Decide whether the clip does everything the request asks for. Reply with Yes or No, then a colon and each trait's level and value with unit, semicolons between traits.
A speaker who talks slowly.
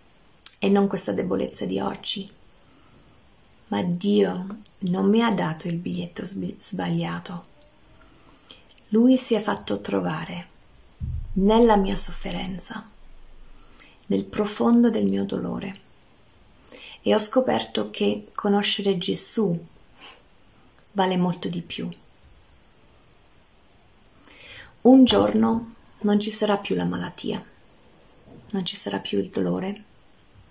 Yes: slow, 100 wpm